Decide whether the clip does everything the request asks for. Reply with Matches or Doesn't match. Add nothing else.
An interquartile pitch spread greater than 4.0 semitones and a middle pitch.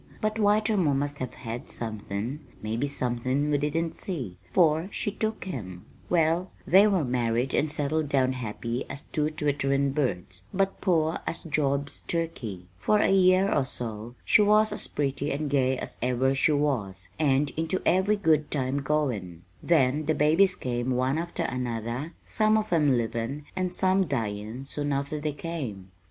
Matches